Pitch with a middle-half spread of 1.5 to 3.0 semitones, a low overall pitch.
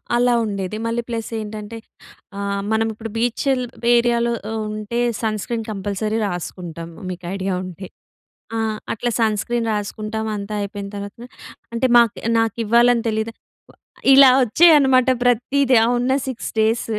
No: average, 2.7 semitones; high, 225 Hz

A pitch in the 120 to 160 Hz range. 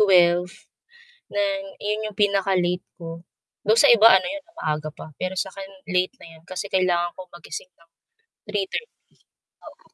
No: medium, 185 Hz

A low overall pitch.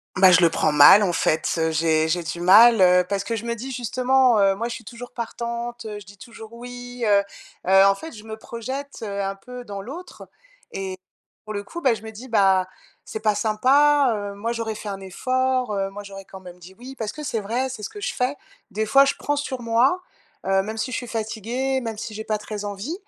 No: high, 220 Hz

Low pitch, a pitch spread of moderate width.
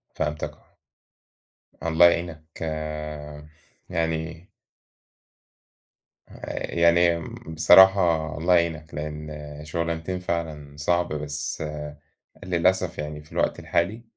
No: very low, 85 Hz; narrow, 2.1 semitones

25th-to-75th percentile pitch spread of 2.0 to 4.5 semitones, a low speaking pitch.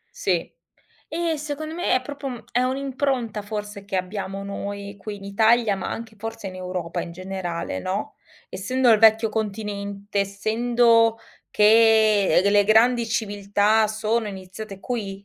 No: narrow, 2.6 semitones; high, 215 Hz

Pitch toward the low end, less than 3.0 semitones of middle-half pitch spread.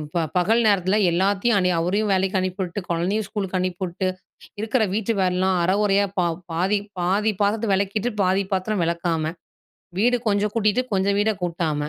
No: high, 195 Hz; narrow, 2.5 semitones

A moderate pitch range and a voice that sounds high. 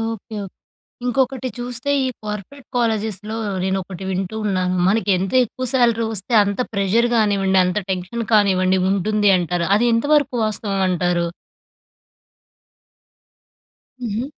Yes: average, 3.6 semitones; high, 210 Hz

